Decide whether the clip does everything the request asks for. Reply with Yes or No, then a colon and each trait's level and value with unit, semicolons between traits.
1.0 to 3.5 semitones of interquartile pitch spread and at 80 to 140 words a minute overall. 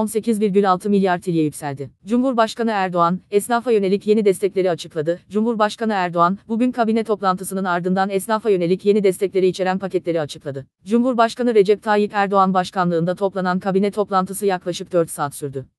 Yes: average, 2.9 semitones; average, 135 wpm